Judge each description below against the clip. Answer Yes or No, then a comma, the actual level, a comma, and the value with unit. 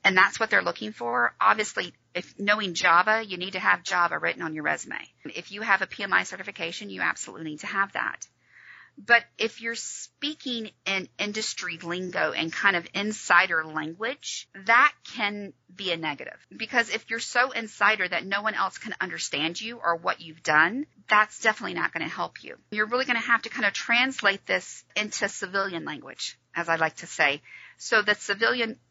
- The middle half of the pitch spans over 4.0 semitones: Yes, average, 4.7 semitones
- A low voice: No, high, 200 Hz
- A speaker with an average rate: Yes, average, 185 wpm